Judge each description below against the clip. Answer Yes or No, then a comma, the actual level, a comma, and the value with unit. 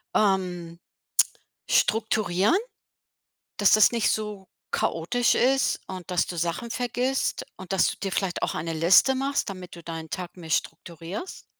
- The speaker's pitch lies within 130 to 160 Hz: No, high, 190 Hz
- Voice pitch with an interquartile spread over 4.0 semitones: Yes, average, 4.6 semitones